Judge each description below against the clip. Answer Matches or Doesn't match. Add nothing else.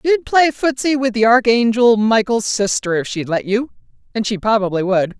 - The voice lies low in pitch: Doesn't match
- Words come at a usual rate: Matches